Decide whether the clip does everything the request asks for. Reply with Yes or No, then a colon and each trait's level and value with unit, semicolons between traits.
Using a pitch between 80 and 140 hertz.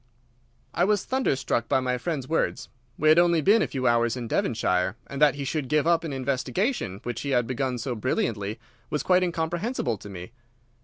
Yes: low, 135 Hz